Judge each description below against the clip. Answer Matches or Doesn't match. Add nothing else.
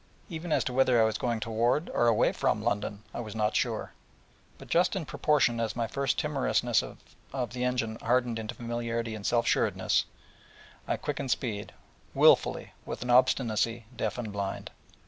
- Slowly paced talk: Doesn't match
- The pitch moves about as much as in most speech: Doesn't match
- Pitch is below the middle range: Matches